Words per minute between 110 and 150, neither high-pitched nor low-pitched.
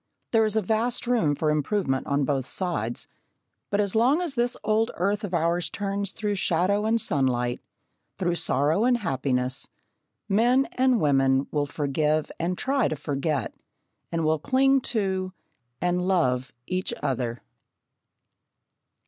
Yes: average, 140 wpm; medium, 180 Hz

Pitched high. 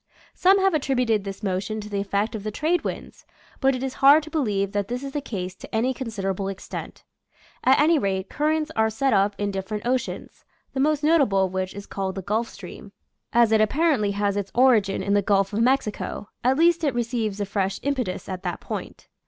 Yes: high, 220 Hz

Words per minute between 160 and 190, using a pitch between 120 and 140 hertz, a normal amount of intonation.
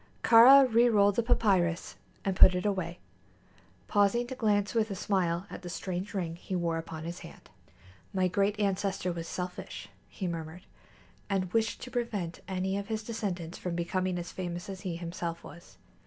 No: average, 170 wpm; medium, 185 Hz; average, 3.1 semitones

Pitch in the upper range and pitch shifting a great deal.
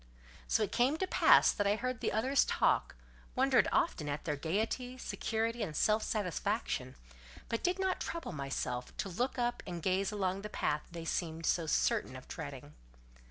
Yes: high, 210 Hz; wide, 6.8 semitones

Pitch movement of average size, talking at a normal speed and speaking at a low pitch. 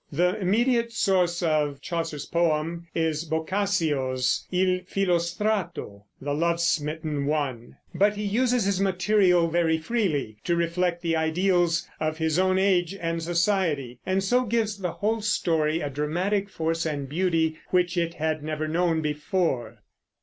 No: average, 3.4 semitones; average, 145 wpm; medium, 170 Hz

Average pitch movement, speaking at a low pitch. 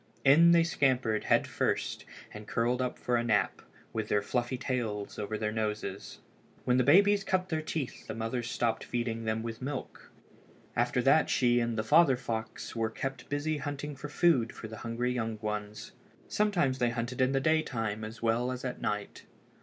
Yes: average, 3.6 semitones; low, 120 Hz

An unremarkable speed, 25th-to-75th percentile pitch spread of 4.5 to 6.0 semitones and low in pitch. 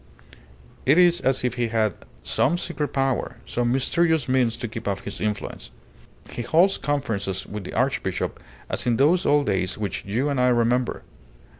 Yes: average, 170 wpm; average, 4.8 semitones; low, 125 Hz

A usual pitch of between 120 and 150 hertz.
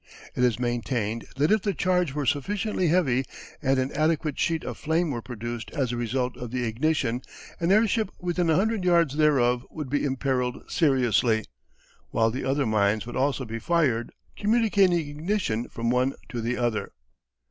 Yes: low, 135 Hz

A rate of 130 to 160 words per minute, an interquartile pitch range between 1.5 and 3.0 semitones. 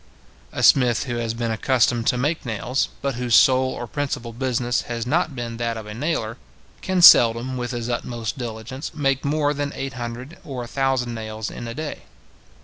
No: average, 190 wpm; average, 2.7 semitones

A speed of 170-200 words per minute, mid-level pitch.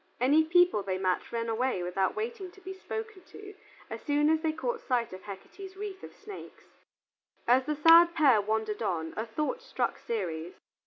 No: average, 180 wpm; very high, 290 Hz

